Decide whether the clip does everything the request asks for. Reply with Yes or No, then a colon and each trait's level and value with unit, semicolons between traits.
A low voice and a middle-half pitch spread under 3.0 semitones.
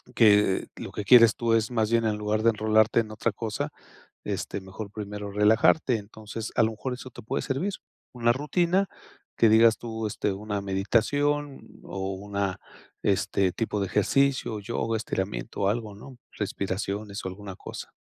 Yes: low, 110 Hz; narrow, 2.4 semitones